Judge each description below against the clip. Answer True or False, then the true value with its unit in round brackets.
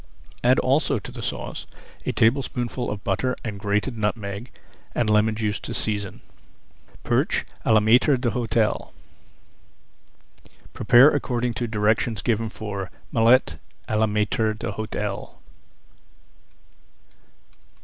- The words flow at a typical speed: False (110 wpm)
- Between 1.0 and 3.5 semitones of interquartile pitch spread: True (2.5 semitones)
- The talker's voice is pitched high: False (110 Hz)